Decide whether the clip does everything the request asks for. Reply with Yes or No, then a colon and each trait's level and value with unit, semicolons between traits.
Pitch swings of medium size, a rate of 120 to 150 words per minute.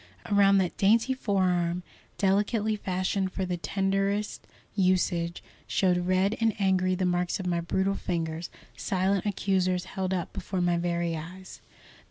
No: narrow, 1.9 semitones; average, 140 wpm